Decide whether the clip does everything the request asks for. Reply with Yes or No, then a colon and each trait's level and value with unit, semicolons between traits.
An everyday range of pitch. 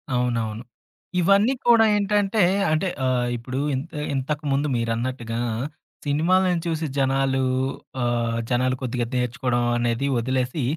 Yes: average, 4.6 semitones